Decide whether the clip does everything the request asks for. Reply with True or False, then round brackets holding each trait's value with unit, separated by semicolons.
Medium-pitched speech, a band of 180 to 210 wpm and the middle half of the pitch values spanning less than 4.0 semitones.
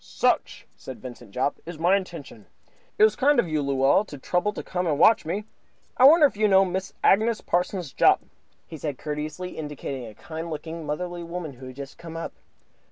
False (165 Hz; 200 wpm; 4.6 semitones)